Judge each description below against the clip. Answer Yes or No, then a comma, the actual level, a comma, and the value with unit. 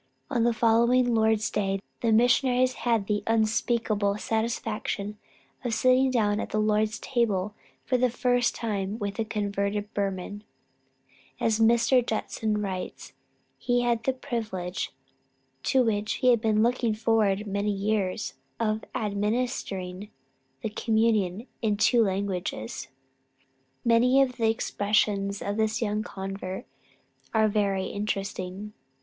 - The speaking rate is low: Yes, slow, 130 wpm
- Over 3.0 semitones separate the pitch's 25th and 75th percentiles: No, narrow, 2.5 semitones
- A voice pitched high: Yes, high, 215 Hz